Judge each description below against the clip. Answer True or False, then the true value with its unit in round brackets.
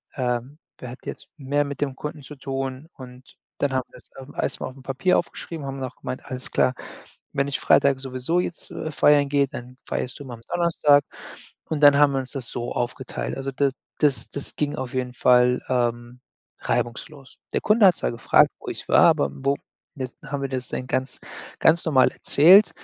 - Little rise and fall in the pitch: True (2.3 semitones)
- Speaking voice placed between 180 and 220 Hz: False (135 Hz)